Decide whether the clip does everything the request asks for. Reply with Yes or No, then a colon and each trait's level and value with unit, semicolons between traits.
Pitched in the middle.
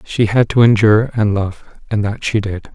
No: low, 105 Hz